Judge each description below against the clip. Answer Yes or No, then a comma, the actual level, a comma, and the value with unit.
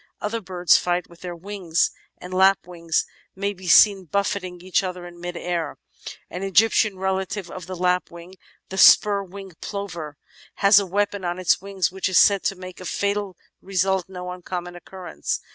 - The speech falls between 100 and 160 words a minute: No, average, 170 wpm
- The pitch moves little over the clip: Yes, narrow, 1.9 semitones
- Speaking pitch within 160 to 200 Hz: Yes, medium, 185 Hz